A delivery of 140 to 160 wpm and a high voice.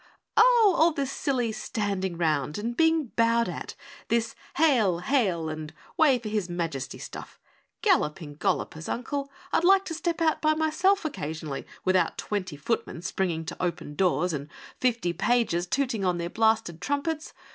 Yes: average, 155 wpm; high, 220 Hz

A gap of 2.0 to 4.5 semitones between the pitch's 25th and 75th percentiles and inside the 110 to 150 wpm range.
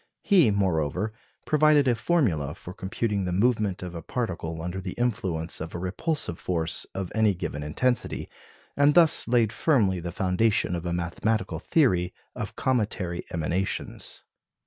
No: wide, 5.5 semitones; average, 145 wpm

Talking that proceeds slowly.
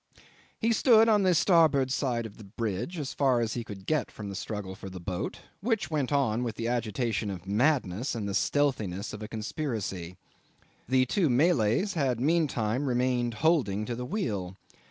No: average, 180 wpm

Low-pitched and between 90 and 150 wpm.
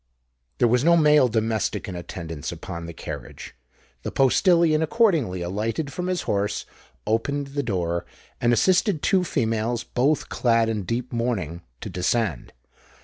Yes: low, 120 Hz; average, 145 wpm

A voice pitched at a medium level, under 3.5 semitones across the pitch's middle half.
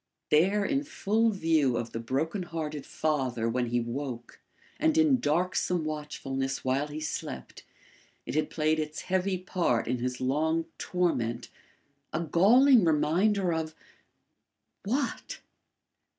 No: medium, 155 Hz; wide, 5.6 semitones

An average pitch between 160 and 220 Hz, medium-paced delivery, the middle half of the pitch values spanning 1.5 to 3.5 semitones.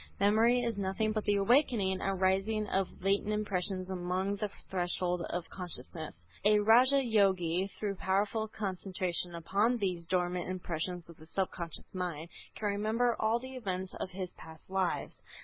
Yes: high, 190 Hz; average, 150 wpm; average, 2.9 semitones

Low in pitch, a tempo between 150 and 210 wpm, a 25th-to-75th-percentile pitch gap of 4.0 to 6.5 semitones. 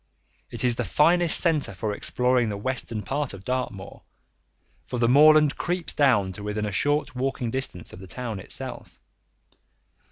Yes: low, 125 Hz; average, 160 wpm; wide, 5.6 semitones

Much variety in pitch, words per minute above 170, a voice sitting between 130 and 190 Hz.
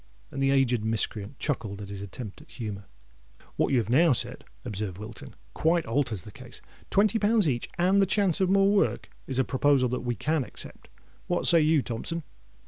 Yes: wide, 7.2 semitones; average, 195 wpm; low, 135 Hz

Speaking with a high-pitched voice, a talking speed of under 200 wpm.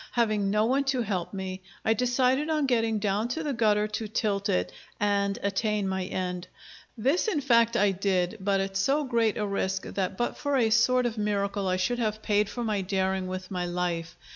No: high, 210 Hz; fast, 205 wpm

